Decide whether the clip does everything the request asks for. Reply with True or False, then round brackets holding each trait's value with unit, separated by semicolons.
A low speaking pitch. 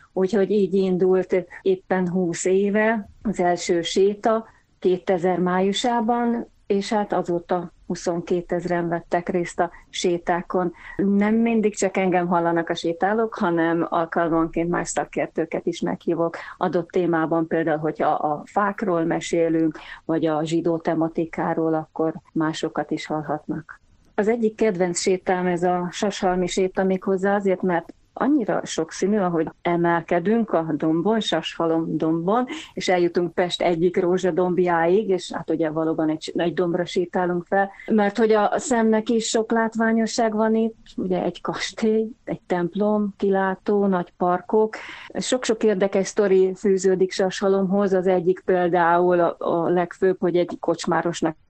False (180 Hz)